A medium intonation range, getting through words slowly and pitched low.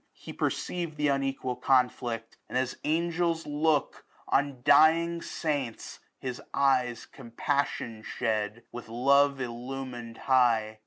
Yes: average, 3.6 semitones; slow, 110 wpm; low, 130 Hz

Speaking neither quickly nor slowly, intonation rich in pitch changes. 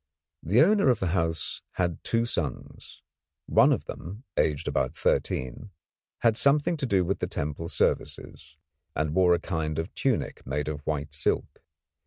Yes: average, 160 wpm; wide, 6.8 semitones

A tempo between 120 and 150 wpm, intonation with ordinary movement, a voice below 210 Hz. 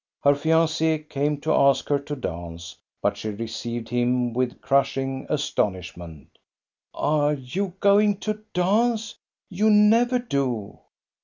No: slow, 135 wpm; wide, 7.3 semitones; medium, 140 Hz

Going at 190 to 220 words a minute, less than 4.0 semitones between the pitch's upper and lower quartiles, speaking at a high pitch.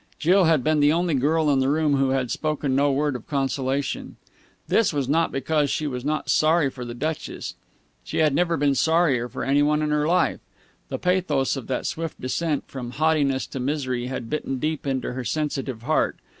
No: average, 200 wpm; average, 2.8 semitones; medium, 145 Hz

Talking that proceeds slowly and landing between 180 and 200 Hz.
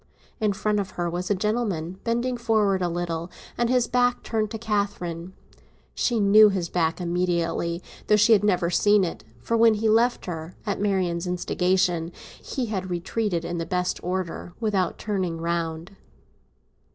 No: average, 165 wpm; high, 190 Hz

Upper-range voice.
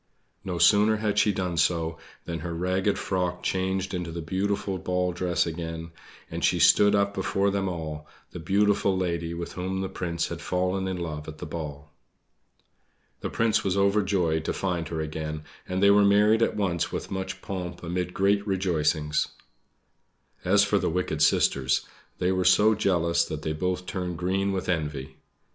No: very low, 90 Hz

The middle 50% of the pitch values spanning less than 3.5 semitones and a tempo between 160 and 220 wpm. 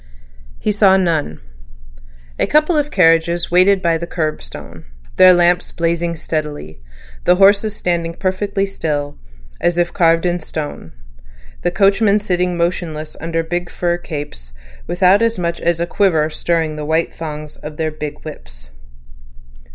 No: average, 2.8 semitones; average, 145 wpm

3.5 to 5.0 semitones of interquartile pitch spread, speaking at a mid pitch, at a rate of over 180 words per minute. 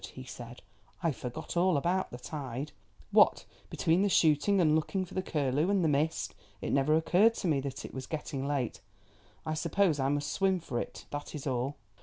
Yes: average, 4.2 semitones; medium, 155 Hz; average, 200 wpm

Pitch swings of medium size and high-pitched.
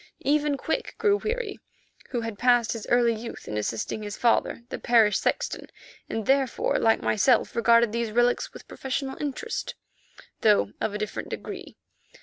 Yes: average, 3.6 semitones; high, 235 Hz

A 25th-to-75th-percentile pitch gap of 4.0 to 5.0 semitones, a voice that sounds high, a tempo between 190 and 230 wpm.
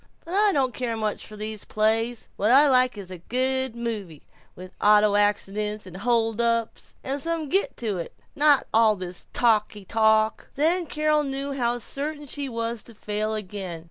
No: average, 4.3 semitones; high, 230 Hz; average, 180 wpm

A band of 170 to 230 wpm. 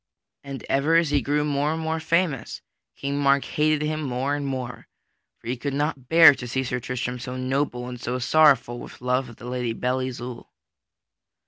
Yes: average, 195 wpm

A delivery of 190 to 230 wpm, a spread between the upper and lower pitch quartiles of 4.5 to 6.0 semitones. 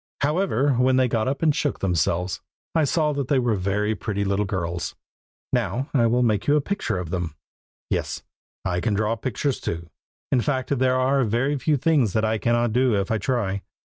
Yes: average, 200 wpm; wide, 5.4 semitones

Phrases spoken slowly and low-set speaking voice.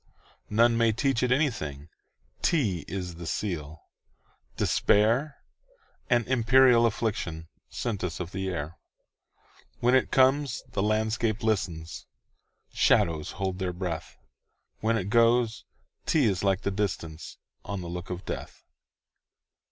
Yes: slow, 105 wpm; low, 105 Hz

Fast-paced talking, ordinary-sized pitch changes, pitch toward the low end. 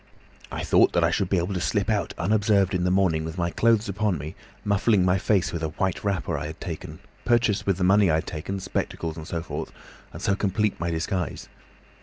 Yes: fast, 225 wpm; average, 3.3 semitones; very low, 95 Hz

